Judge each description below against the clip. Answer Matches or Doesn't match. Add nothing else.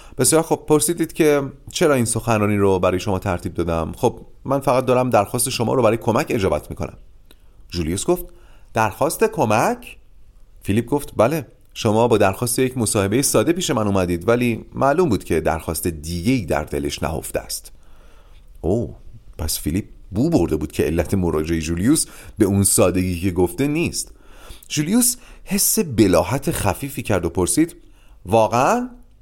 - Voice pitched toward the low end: Matches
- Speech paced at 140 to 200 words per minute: Matches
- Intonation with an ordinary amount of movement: Doesn't match